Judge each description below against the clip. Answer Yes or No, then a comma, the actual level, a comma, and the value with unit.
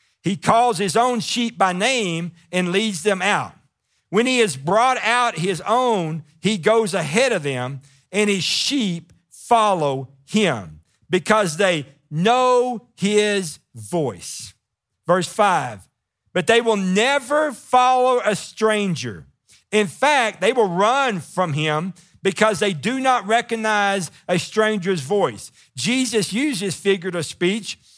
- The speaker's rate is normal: No, slow, 130 wpm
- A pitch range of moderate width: No, wide, 5.8 semitones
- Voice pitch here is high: Yes, high, 195 Hz